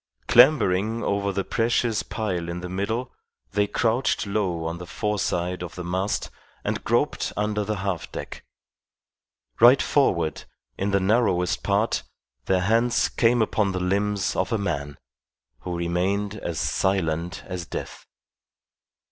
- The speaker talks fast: No, average, 140 wpm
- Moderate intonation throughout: Yes, average, 3.2 semitones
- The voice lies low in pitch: Yes, low, 100 Hz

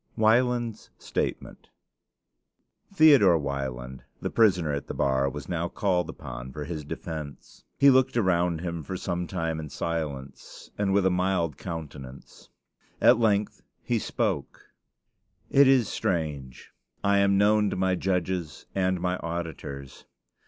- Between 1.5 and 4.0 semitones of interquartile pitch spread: No, average, 5.1 semitones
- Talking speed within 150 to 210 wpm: No, slow, 135 wpm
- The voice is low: Yes, very low, 85 Hz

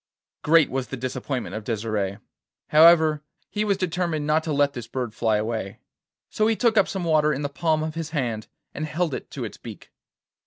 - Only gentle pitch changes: No, wide, 5.4 semitones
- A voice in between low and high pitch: Yes, medium, 150 Hz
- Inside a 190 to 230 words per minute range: Yes, average, 200 wpm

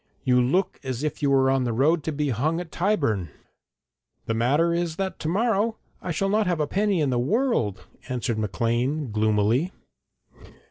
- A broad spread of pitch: Yes, wide, 6.6 semitones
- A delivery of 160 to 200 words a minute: Yes, average, 180 wpm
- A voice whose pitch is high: No, medium, 145 Hz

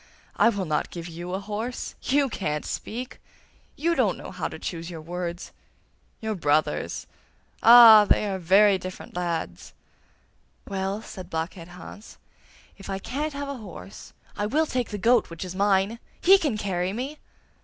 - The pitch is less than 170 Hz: No, high, 195 Hz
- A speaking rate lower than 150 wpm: No, average, 165 wpm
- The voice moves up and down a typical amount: Yes, average, 4.8 semitones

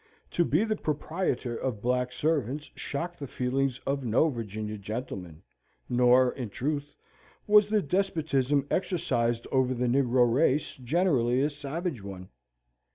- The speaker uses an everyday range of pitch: Yes, average, 4.0 semitones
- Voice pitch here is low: Yes, low, 130 Hz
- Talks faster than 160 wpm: No, slow, 135 wpm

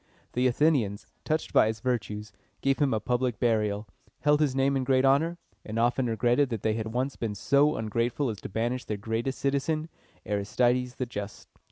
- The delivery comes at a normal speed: Yes, average, 185 wpm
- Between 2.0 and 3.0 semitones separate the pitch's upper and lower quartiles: No, average, 3.7 semitones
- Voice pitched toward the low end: Yes, low, 125 Hz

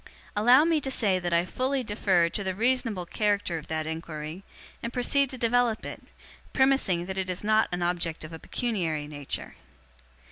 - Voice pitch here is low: No, high, 195 Hz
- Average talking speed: Yes, average, 180 wpm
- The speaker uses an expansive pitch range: Yes, wide, 6.2 semitones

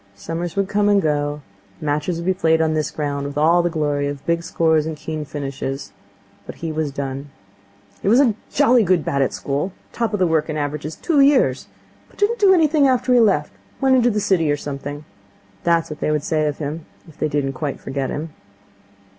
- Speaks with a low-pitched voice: No, medium, 155 Hz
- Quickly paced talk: Yes, fast, 215 wpm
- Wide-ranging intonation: No, average, 5.0 semitones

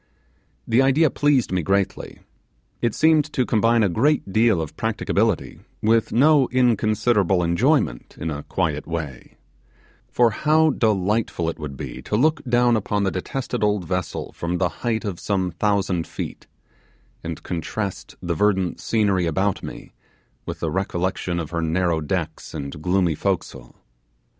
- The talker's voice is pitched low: Yes, very low, 95 Hz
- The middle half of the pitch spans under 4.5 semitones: No, average, 5.3 semitones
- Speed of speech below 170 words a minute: Yes, average, 150 wpm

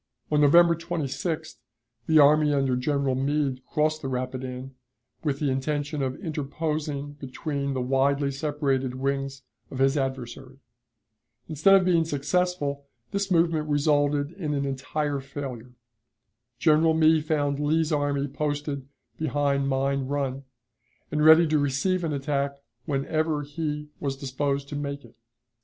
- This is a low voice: No, medium, 145 Hz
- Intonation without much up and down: Yes, narrow, 2.1 semitones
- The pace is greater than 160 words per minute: No, slow, 135 wpm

